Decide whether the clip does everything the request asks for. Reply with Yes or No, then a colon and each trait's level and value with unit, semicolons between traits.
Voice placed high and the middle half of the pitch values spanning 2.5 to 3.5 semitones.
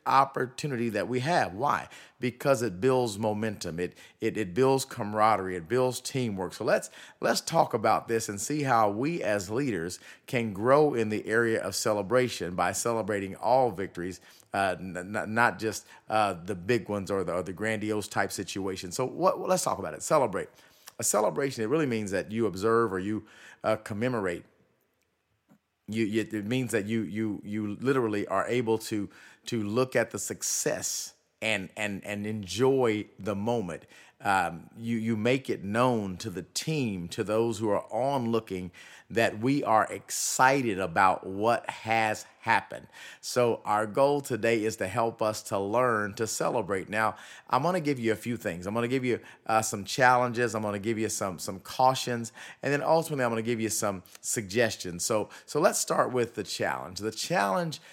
No: low, 110 Hz; average, 3.1 semitones